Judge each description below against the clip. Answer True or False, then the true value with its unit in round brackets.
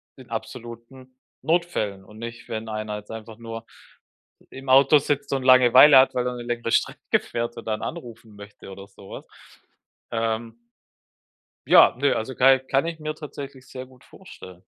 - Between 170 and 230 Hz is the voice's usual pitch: False (120 Hz)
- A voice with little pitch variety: False (3.1 semitones)